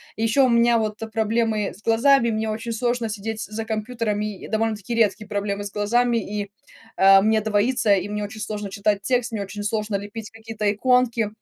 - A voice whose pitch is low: No, high, 220 Hz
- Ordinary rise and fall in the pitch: No, narrow, 1.9 semitones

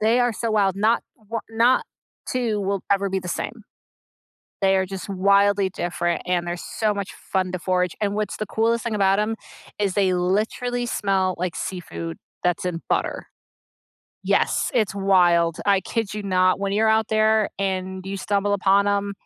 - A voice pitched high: Yes, high, 200 Hz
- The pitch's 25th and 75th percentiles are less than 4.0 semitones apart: Yes, narrow, 2.5 semitones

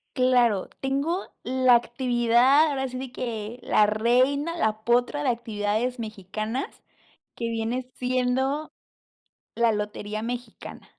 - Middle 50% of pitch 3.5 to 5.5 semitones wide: No, average, 2.8 semitones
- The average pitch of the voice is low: No, high, 245 Hz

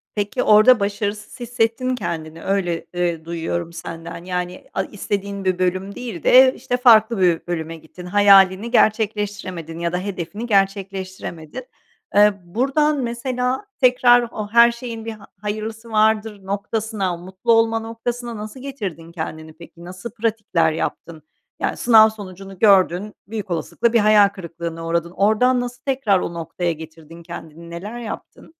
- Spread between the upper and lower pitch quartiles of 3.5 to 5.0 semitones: Yes, average, 4.7 semitones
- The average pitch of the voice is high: Yes, high, 200 Hz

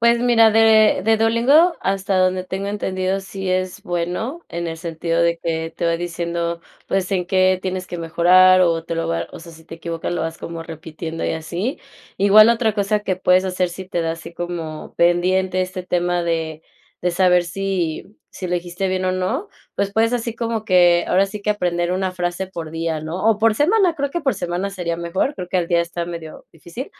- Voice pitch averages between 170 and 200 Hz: Yes, medium, 185 Hz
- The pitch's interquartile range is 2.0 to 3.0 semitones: Yes, average, 2.7 semitones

